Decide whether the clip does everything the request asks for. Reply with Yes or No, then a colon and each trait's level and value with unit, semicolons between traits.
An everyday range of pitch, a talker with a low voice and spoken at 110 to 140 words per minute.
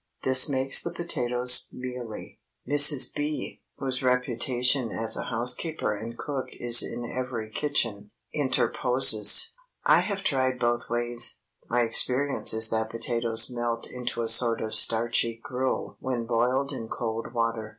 No: narrow, 2.3 semitones; low, 120 Hz; slow, 135 wpm